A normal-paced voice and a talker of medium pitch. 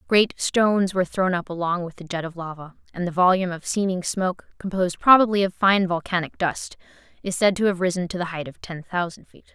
No: fast, 220 wpm; medium, 180 Hz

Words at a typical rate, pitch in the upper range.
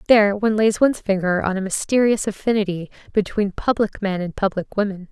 Yes: average, 175 wpm; high, 205 Hz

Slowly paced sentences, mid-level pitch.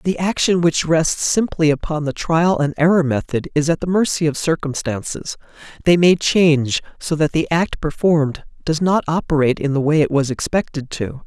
No: average, 185 wpm; medium, 155 Hz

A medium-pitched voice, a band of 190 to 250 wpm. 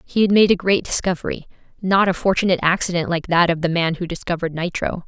Yes: medium, 175 Hz; average, 200 wpm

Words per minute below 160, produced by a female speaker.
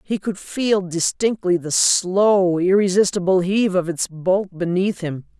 Yes: average, 145 wpm; female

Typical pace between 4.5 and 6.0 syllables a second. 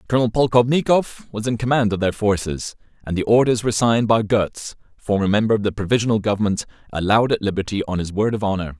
No: 6.7 syllables/s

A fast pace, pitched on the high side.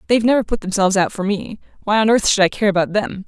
Yes: fast, 255 wpm; high, 205 Hz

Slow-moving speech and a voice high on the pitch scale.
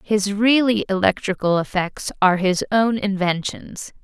Yes: slow, 120 wpm; high, 200 Hz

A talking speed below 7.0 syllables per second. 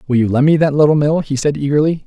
Yes: 6.8 syllables/s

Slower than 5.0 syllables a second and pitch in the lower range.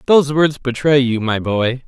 Yes: 4.7 syllables/s; low, 130 Hz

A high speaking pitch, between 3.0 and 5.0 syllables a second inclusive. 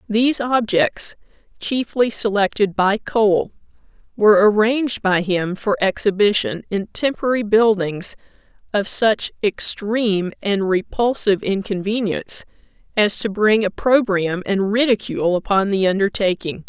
Yes: high, 205 Hz; 4.5 syllables/s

